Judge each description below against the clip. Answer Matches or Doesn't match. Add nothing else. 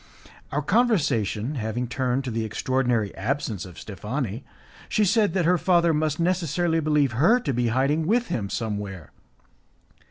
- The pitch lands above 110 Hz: Matches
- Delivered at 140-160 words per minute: Matches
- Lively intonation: Matches